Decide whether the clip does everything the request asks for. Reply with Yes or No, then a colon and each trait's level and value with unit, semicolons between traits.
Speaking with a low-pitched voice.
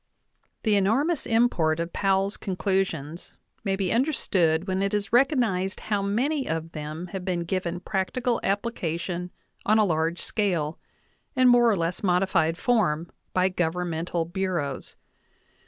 No: high, 190 Hz